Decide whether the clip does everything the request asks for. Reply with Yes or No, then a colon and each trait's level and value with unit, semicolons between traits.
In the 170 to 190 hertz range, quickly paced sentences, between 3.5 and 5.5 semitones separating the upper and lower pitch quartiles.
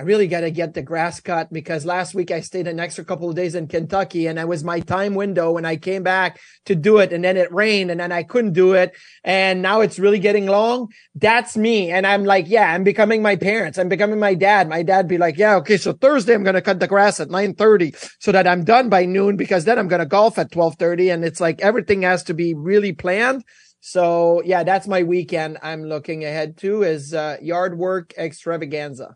No: medium, 185 Hz; fast, 235 wpm; average, 3.0 semitones